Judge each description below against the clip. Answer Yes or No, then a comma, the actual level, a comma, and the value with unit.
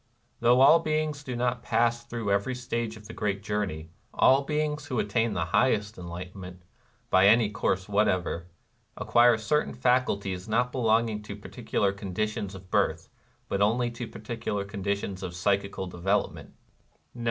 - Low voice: Yes, low, 105 Hz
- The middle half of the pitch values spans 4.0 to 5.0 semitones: No, average, 3.6 semitones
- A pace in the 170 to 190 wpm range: No, average, 150 wpm